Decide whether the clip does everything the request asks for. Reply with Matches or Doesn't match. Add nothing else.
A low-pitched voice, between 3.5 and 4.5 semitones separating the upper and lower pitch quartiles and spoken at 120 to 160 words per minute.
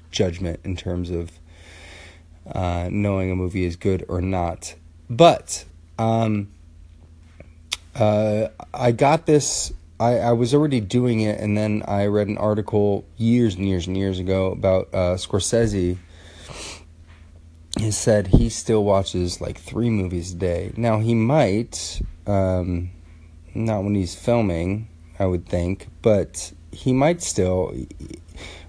Matches